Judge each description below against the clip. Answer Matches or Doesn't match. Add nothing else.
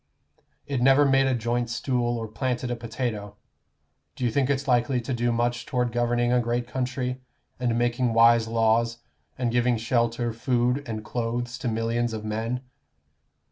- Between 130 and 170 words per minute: Matches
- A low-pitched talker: Matches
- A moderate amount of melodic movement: Doesn't match